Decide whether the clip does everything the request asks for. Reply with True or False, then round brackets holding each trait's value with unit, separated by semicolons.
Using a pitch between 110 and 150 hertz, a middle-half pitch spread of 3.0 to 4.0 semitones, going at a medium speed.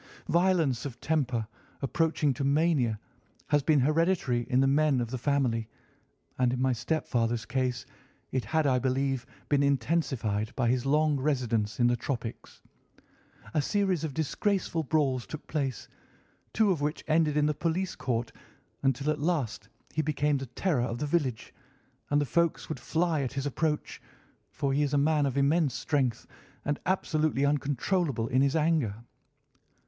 True (140 Hz; 3.7 semitones; 160 wpm)